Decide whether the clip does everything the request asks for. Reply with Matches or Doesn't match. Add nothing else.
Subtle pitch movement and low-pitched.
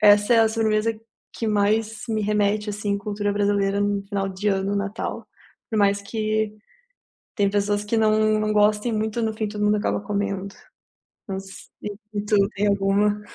Doesn't match